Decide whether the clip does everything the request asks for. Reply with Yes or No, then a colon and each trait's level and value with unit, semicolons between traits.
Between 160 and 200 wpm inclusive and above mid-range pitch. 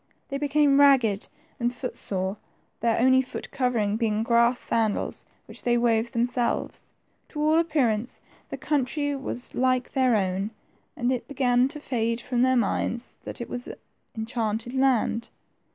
No: average, 150 wpm; high, 245 Hz